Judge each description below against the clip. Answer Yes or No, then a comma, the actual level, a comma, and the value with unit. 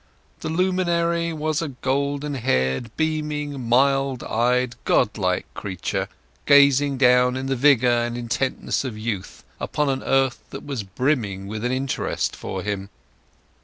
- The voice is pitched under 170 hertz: Yes, low, 135 Hz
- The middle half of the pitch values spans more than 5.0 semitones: No, average, 3.5 semitones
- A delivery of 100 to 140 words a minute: Yes, slow, 135 wpm